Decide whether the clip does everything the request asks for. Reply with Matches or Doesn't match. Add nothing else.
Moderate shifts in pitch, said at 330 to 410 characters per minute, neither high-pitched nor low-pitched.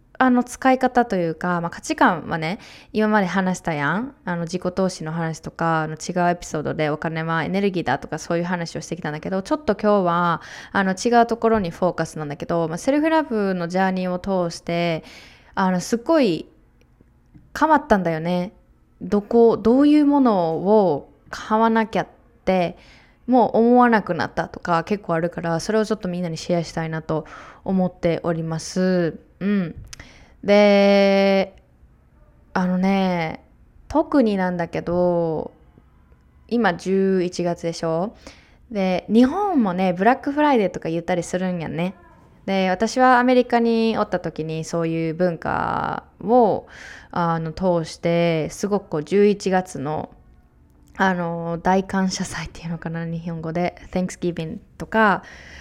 Doesn't match